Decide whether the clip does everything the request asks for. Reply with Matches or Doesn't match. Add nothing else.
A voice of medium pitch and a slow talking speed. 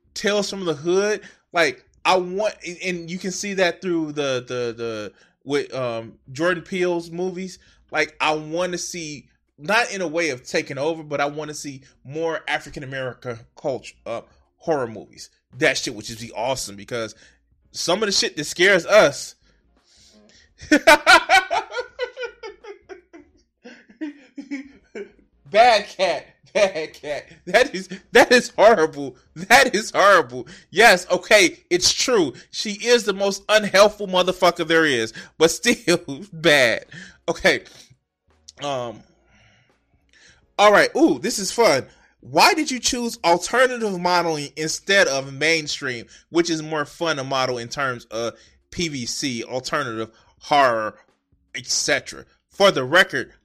Matches